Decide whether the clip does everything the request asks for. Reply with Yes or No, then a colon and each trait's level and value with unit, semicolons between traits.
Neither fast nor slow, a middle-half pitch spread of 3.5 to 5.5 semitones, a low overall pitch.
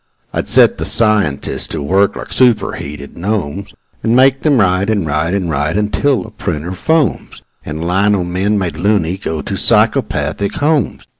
Yes: average, 160 wpm; average, 4.8 semitones; very low, 95 Hz